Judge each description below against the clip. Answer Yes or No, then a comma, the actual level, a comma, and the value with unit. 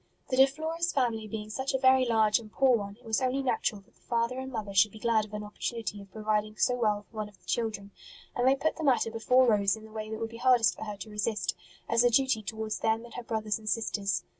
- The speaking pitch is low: No, high, 220 Hz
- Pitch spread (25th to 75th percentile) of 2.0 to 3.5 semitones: Yes, average, 2.9 semitones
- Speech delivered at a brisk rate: Yes, fast, 265 wpm